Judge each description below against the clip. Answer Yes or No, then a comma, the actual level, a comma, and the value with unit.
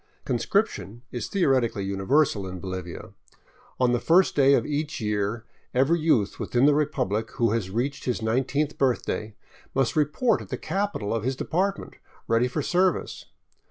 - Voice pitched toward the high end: No, low, 125 Hz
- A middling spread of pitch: No, wide, 5.7 semitones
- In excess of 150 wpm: Yes, average, 160 wpm